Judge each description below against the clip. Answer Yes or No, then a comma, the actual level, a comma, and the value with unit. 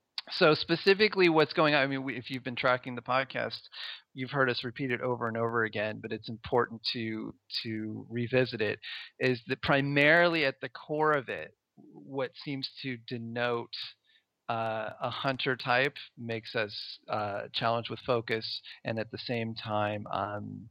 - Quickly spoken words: No, average, 170 wpm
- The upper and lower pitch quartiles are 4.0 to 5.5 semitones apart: No, average, 3.0 semitones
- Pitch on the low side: Yes, low, 125 Hz